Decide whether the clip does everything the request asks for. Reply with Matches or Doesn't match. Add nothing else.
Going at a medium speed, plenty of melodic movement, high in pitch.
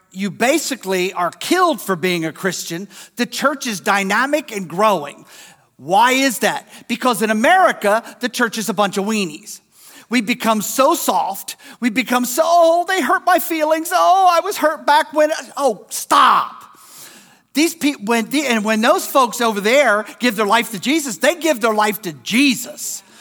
Matches